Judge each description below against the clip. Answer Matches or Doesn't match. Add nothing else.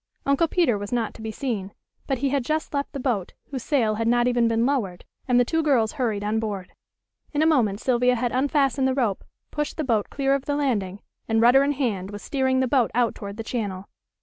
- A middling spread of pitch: Matches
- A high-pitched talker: Matches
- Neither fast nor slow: Doesn't match